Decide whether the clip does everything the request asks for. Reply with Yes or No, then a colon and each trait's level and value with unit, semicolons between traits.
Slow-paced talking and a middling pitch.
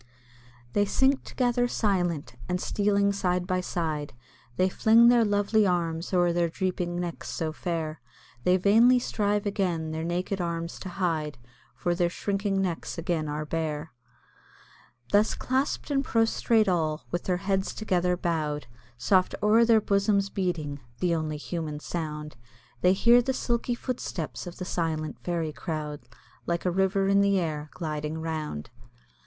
No: average, 150 wpm; medium, 180 Hz